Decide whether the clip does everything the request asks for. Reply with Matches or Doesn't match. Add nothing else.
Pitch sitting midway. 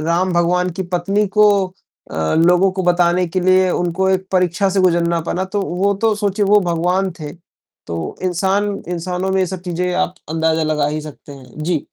Matches